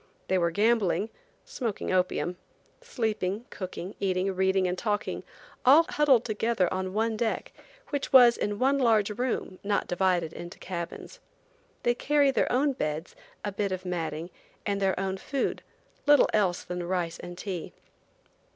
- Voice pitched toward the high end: Yes, high, 200 Hz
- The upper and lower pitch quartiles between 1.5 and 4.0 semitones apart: No, average, 4.6 semitones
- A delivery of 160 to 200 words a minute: No, average, 150 wpm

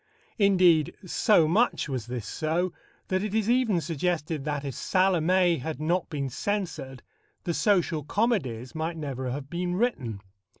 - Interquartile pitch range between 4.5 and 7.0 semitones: Yes, average, 5.0 semitones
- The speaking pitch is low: No, medium, 165 Hz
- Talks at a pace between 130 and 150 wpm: Yes, average, 145 wpm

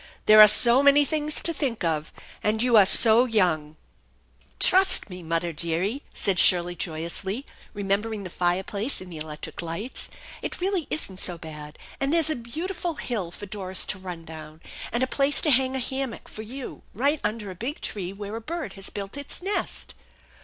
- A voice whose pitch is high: Yes, high, 210 Hz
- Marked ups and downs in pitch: Yes, wide, 7.2 semitones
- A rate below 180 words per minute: No, average, 195 wpm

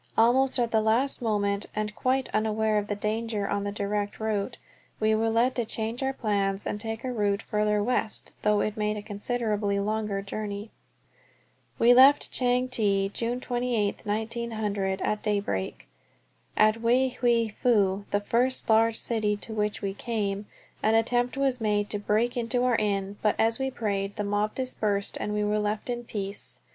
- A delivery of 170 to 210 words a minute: Yes, average, 175 wpm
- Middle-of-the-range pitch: No, high, 215 Hz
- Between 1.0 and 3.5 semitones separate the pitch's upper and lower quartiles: Yes, narrow, 2.4 semitones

